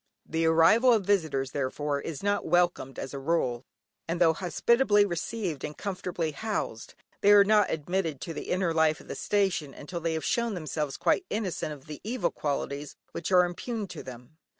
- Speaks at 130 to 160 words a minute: No, average, 185 wpm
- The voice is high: No, medium, 170 Hz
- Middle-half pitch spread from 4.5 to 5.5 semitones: Yes, average, 5.1 semitones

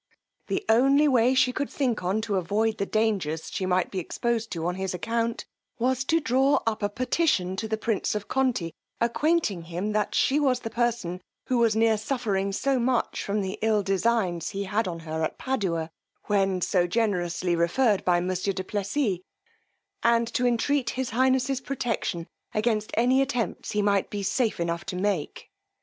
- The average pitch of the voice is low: No, high, 215 Hz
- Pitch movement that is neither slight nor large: Yes, average, 4.7 semitones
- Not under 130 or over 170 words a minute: No, average, 180 wpm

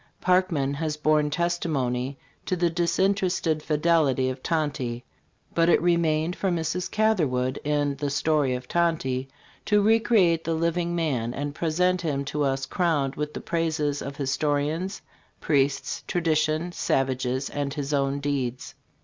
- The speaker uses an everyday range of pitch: Yes, average, 3.6 semitones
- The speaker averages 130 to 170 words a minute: Yes, average, 140 wpm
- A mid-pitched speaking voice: Yes, medium, 150 Hz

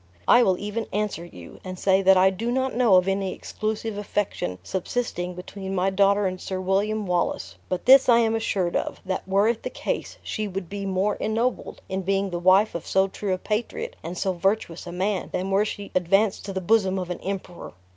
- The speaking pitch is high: Yes, high, 195 Hz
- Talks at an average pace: No, fast, 215 wpm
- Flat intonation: Yes, narrow, 2.3 semitones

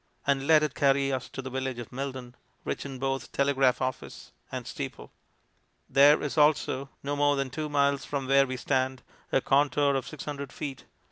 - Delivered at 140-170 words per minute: No, average, 185 wpm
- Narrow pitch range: Yes, narrow, 1.4 semitones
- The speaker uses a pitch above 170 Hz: No, low, 135 Hz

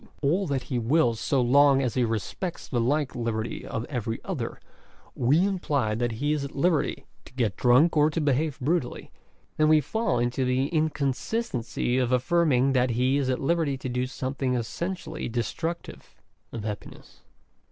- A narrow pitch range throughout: No, average, 4.0 semitones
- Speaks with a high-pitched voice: No, low, 135 Hz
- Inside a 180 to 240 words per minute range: No, average, 165 wpm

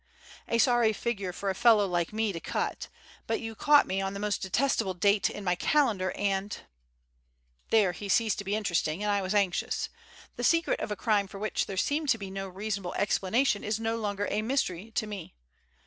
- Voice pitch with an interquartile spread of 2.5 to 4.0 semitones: Yes, average, 2.8 semitones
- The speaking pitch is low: No, high, 205 Hz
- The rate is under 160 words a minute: No, average, 200 wpm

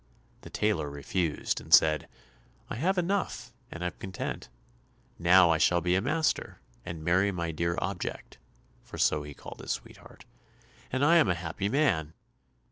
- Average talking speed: Yes, average, 160 wpm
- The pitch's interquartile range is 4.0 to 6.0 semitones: Yes, average, 4.7 semitones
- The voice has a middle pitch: No, very low, 90 Hz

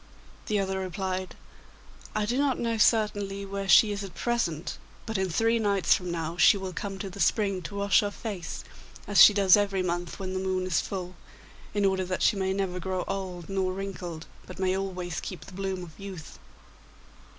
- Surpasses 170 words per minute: Yes, average, 195 wpm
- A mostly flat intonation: Yes, narrow, 1.6 semitones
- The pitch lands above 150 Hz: Yes, high, 190 Hz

